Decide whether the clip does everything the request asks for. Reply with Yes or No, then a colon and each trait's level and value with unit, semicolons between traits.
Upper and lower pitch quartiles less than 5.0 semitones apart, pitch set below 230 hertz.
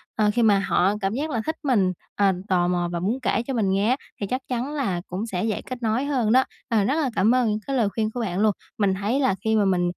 Yes: average, 4.5 semitones; high, 220 Hz